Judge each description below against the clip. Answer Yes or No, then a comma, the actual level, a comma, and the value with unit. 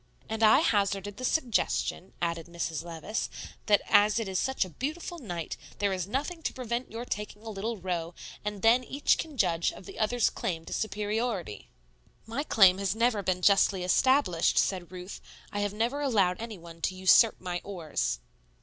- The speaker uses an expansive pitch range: No, average, 4.3 semitones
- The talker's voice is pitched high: Yes, high, 205 Hz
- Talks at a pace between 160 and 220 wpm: Yes, average, 180 wpm